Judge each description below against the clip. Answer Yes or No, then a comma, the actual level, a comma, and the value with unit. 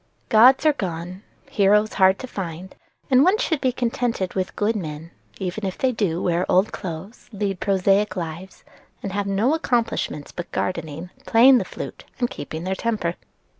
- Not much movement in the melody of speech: No, average, 4.3 semitones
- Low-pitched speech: No, high, 195 Hz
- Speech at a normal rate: Yes, average, 170 wpm